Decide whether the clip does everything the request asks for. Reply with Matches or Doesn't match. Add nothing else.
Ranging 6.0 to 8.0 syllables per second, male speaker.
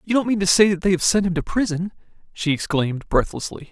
Matches